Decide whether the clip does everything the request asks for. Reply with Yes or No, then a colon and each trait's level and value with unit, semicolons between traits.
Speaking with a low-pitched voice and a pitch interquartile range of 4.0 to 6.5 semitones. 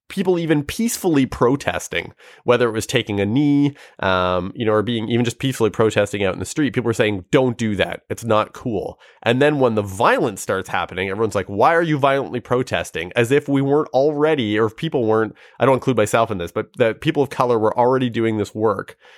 Yes: low, 120 Hz; average, 4.3 semitones